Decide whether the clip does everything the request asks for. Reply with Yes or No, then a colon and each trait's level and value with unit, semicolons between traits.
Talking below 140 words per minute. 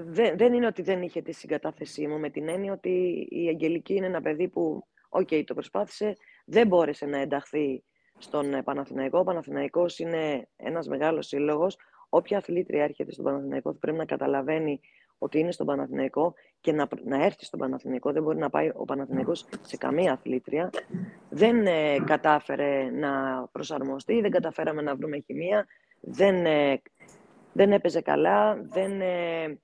No: average, 150 wpm